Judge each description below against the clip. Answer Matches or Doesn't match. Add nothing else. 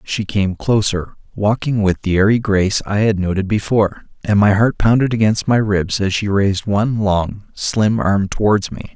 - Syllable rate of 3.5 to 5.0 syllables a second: Matches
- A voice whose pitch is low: Matches